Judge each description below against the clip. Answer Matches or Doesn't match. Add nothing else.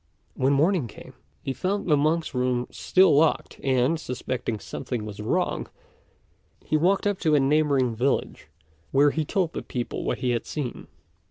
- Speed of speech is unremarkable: Matches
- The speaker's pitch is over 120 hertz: Matches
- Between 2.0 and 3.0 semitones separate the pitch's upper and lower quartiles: Doesn't match